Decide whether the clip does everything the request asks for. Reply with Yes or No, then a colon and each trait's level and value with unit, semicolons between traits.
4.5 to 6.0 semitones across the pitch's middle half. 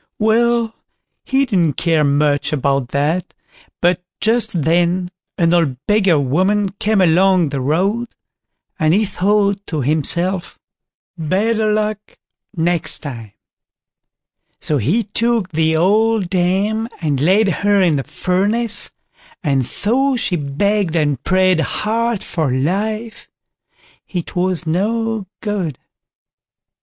Yes: average, 5.1 semitones